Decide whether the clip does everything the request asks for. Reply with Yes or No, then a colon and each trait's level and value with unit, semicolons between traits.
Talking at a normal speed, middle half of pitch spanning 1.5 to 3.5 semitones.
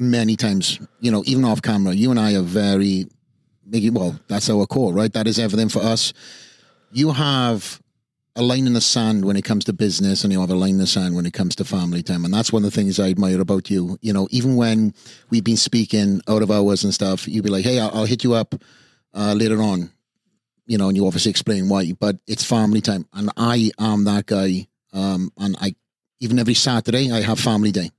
No: fast, 230 wpm; average, 2.9 semitones